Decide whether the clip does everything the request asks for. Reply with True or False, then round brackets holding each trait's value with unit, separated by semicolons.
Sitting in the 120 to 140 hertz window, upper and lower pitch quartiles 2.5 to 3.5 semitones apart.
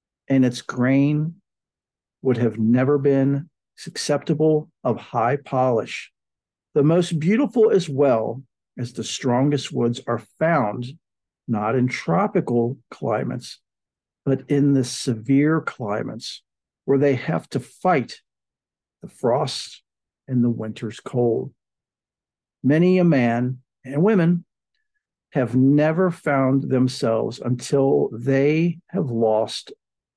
False (135 Hz; 4.3 semitones)